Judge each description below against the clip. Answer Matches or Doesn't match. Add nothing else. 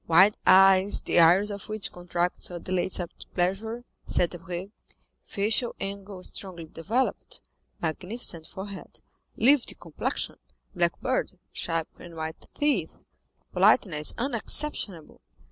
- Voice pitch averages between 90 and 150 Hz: Doesn't match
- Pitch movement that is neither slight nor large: Matches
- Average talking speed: Doesn't match